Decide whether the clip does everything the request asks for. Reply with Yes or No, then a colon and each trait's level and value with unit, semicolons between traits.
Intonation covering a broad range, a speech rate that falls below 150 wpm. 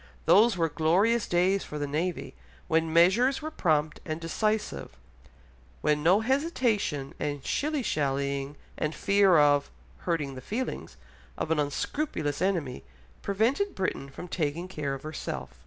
Yes: wide, 5.9 semitones; average, 140 wpm